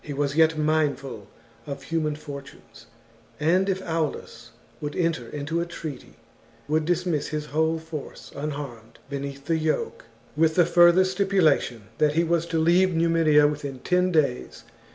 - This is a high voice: No, medium, 155 Hz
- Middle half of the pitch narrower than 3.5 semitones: Yes, average, 2.7 semitones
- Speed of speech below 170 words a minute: Yes, average, 145 wpm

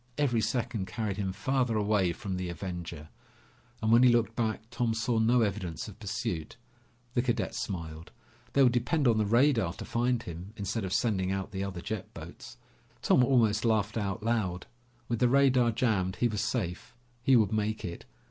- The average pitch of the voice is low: Yes, low, 110 Hz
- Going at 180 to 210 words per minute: Yes, average, 185 wpm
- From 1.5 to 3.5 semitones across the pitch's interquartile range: No, average, 4.0 semitones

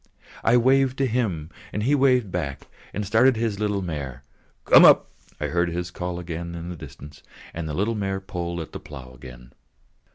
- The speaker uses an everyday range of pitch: No, wide, 5.8 semitones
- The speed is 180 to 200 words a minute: Yes, average, 195 wpm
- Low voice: Yes, very low, 90 Hz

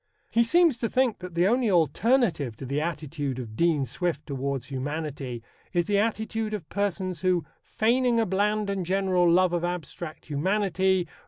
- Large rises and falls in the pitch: Yes, wide, 5.7 semitones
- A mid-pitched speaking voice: Yes, medium, 180 Hz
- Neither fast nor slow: Yes, average, 165 wpm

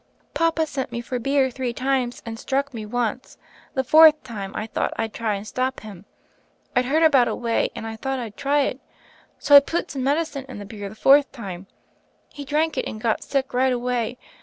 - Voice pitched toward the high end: Yes, very high, 255 Hz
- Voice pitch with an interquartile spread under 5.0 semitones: Yes, average, 3.8 semitones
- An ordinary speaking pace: No, fast, 210 wpm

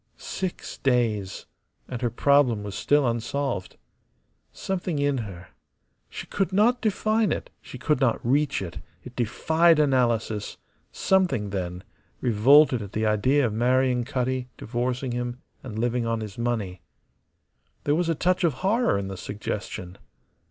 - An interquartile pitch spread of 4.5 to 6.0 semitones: Yes, average, 5.1 semitones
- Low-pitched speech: Yes, low, 125 Hz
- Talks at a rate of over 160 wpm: No, average, 145 wpm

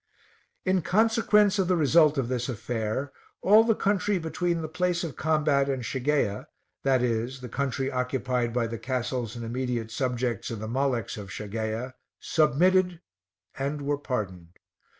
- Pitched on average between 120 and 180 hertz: Yes, low, 135 Hz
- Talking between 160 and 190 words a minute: No, average, 150 wpm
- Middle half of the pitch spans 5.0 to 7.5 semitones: Yes, wide, 5.5 semitones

